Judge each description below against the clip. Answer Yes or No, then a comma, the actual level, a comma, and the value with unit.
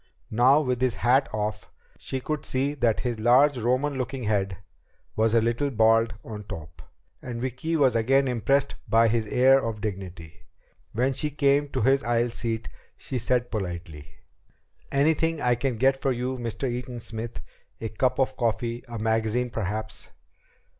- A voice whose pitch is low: Yes, low, 120 Hz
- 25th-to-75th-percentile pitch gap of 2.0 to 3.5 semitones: Yes, average, 3.1 semitones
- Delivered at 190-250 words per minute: No, average, 160 wpm